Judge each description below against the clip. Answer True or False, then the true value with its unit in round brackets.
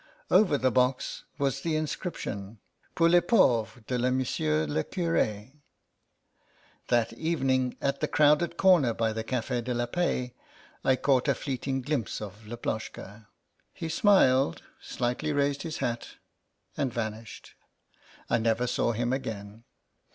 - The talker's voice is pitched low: True (125 Hz)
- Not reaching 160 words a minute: True (135 wpm)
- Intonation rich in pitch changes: False (4.2 semitones)